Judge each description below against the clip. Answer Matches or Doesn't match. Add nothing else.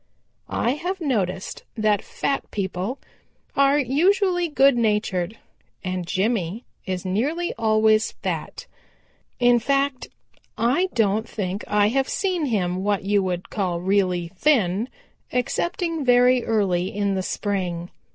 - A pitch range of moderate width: Doesn't match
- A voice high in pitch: Matches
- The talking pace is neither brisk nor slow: Doesn't match